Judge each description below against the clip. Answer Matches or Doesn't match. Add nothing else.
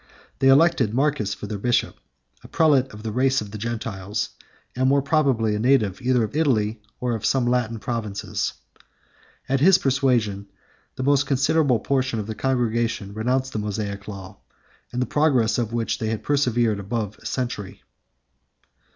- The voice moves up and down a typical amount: Matches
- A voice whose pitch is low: Matches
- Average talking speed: Matches